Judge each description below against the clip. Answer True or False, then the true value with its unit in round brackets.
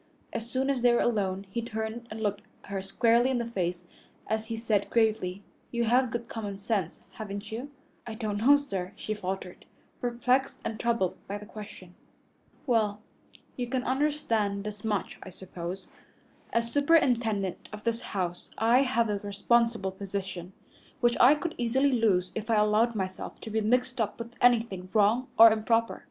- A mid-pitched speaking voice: False (220 Hz)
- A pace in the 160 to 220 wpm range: True (170 wpm)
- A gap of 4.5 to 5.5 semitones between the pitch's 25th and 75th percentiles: False (3.0 semitones)